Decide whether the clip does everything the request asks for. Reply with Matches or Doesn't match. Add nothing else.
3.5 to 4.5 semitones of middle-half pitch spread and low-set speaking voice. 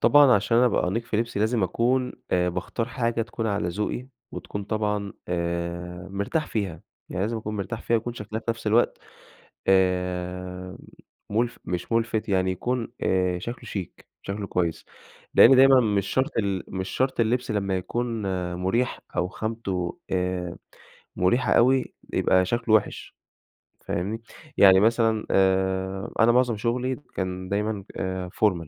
Matches